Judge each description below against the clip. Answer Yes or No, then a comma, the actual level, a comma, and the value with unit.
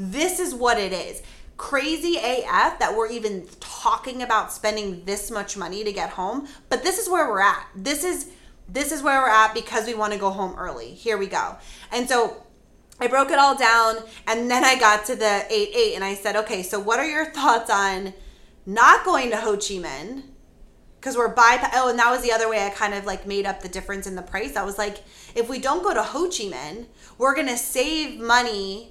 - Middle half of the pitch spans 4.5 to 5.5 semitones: Yes, average, 4.8 semitones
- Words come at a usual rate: No, fast, 225 wpm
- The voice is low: No, high, 230 Hz